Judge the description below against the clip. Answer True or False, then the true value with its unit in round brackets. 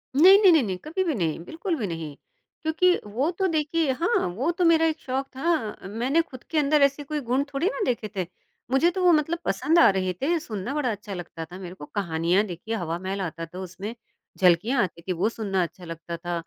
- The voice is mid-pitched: False (235 Hz)